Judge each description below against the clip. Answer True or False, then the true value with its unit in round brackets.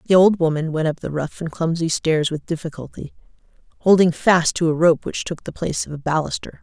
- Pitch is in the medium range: True (160 Hz)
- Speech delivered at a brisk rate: True (210 wpm)